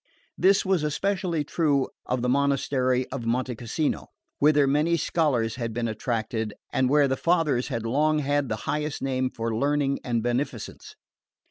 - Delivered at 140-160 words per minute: Yes, average, 155 wpm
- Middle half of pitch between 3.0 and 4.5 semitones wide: Yes, average, 3.7 semitones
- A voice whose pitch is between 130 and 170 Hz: Yes, low, 135 Hz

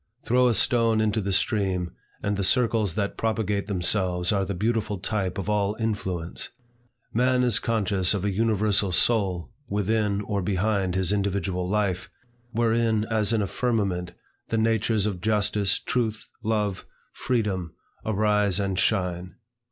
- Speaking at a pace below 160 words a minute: Yes, average, 145 wpm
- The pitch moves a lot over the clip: No, average, 2.7 semitones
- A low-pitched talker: Yes, low, 105 Hz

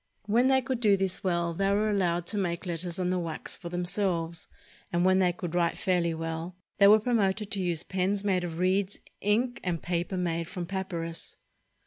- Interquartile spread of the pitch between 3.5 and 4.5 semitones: No, average, 2.7 semitones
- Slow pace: No, average, 195 wpm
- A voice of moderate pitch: Yes, medium, 180 Hz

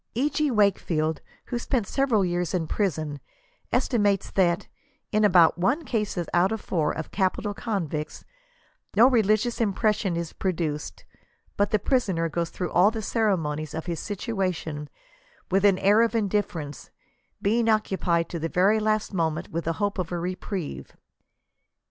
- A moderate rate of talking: Yes, average, 160 wpm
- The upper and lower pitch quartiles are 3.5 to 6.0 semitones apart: Yes, average, 4.4 semitones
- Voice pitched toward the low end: No, high, 190 Hz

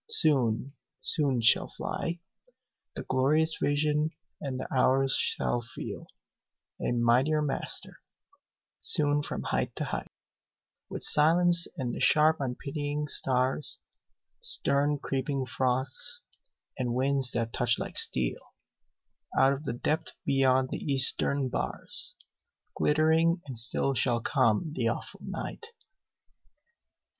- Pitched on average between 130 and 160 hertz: Yes, low, 135 Hz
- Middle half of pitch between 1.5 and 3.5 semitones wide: Yes, average, 2.8 semitones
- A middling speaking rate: No, slow, 115 wpm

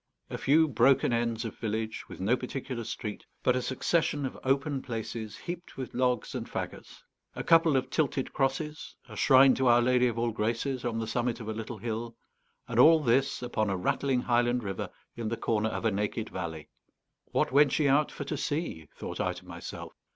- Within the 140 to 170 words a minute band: No, average, 200 wpm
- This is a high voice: No, low, 120 Hz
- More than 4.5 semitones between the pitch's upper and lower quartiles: No, average, 3.2 semitones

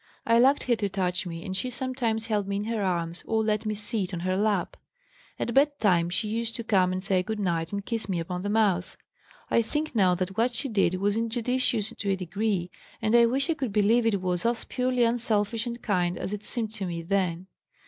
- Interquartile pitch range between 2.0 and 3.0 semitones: No, average, 3.9 semitones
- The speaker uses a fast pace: Yes, fast, 230 wpm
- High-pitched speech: Yes, high, 210 Hz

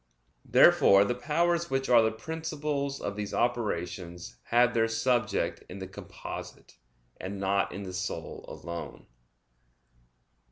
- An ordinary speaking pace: No, slow, 125 wpm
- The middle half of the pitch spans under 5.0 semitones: No, wide, 5.5 semitones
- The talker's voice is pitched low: Yes, low, 115 Hz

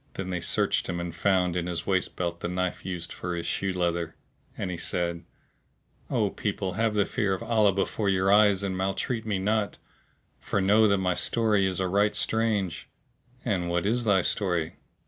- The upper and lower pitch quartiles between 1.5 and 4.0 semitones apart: Yes, average, 2.7 semitones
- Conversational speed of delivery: Yes, average, 190 wpm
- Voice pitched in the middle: No, very low, 95 Hz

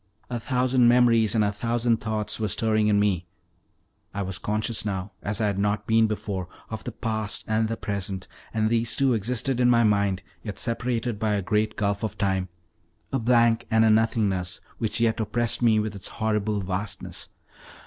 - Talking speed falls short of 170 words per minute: No, average, 185 wpm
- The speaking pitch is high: No, low, 110 Hz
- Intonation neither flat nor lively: No, narrow, 2.2 semitones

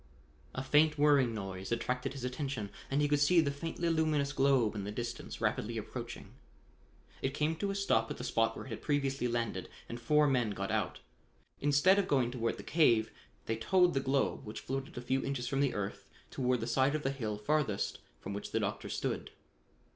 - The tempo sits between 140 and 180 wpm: No, fast, 205 wpm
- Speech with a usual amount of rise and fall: Yes, average, 4.0 semitones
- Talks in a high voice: No, low, 135 Hz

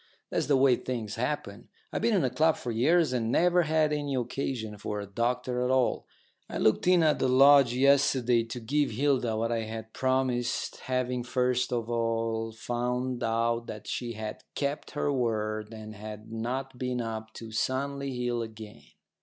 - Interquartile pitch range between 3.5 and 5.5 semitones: No, average, 2.9 semitones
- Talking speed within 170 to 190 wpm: Yes, average, 180 wpm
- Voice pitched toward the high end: No, low, 125 Hz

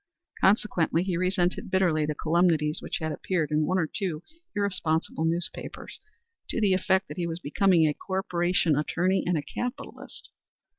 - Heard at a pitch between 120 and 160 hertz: No, medium, 175 Hz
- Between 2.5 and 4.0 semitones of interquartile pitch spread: Yes, average, 3.0 semitones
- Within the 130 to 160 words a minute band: Yes, average, 155 wpm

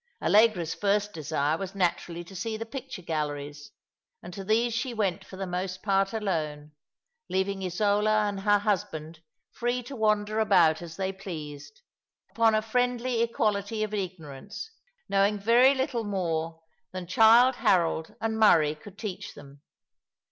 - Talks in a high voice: Yes, high, 200 Hz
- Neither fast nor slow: Yes, average, 150 wpm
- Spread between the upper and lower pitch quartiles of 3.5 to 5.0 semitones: Yes, average, 4.6 semitones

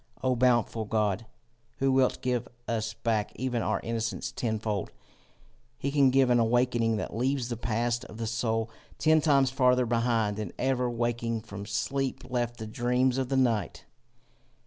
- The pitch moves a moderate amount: No, narrow, 2.3 semitones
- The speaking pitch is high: No, low, 120 Hz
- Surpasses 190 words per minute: No, average, 160 wpm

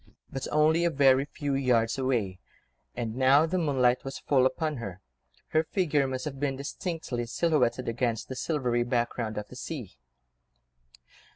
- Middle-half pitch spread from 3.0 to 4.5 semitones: Yes, average, 3.6 semitones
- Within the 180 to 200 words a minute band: No, average, 155 wpm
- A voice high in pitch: No, low, 130 Hz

